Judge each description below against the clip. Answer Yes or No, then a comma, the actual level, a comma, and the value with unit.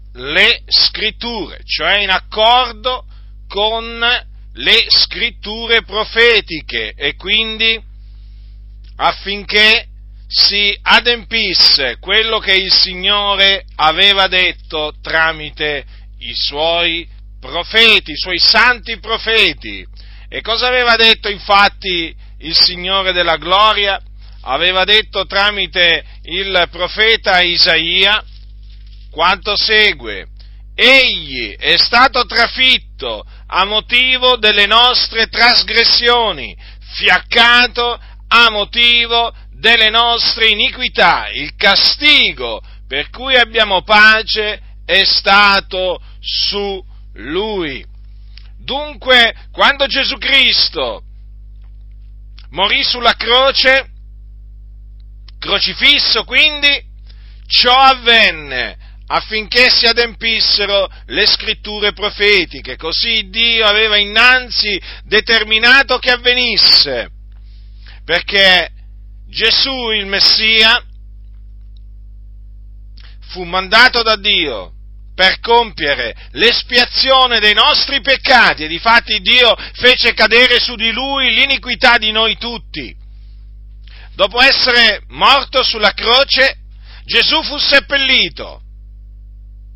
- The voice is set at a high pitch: Yes, high, 205 Hz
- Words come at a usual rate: No, slow, 85 wpm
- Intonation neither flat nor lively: No, wide, 8.2 semitones